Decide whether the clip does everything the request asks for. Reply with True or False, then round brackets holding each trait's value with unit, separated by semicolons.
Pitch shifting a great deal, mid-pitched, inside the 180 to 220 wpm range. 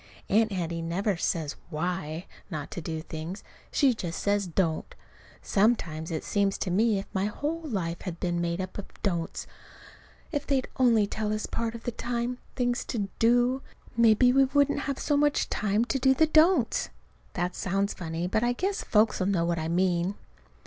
False (5.9 semitones; 200 Hz; 185 wpm)